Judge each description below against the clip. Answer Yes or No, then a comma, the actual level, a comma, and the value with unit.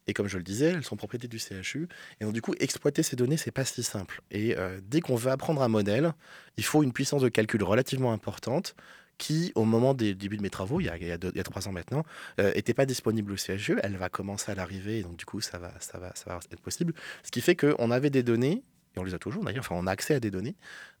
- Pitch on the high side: No, low, 110 Hz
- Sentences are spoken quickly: Yes, fast, 290 wpm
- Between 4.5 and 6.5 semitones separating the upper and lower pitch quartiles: Yes, average, 5.1 semitones